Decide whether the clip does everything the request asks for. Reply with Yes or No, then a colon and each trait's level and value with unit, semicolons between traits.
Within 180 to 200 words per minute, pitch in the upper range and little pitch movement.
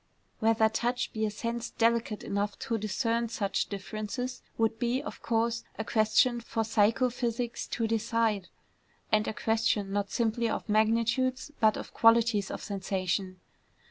No: average, 145 wpm; high, 225 Hz; narrow, 1.7 semitones